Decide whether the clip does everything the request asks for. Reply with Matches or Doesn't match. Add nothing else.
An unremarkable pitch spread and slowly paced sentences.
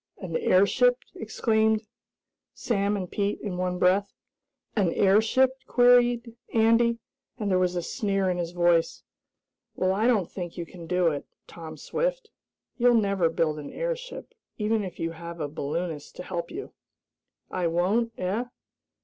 Doesn't match